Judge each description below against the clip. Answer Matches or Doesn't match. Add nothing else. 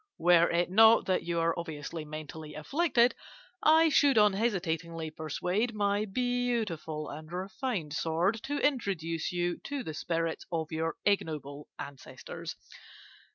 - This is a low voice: Doesn't match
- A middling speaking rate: Doesn't match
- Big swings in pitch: Matches